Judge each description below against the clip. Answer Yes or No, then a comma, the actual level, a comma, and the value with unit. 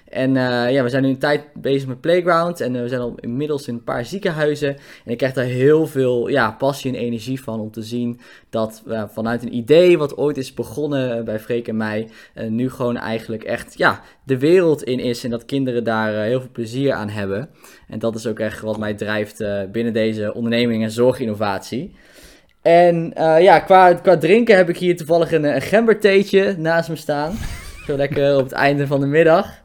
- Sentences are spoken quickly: Yes, fast, 215 wpm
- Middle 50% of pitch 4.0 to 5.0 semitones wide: Yes, average, 4.7 semitones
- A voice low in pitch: Yes, low, 130 Hz